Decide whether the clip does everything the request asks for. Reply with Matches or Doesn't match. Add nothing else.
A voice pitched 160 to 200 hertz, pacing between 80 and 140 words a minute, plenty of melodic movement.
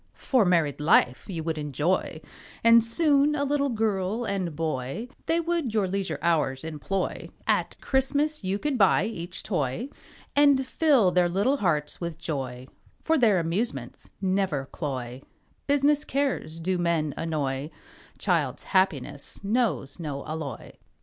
Matches